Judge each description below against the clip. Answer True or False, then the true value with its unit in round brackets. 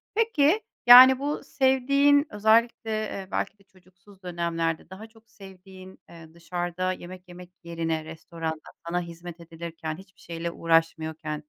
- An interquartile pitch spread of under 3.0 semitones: False (4.6 semitones)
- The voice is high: False (180 Hz)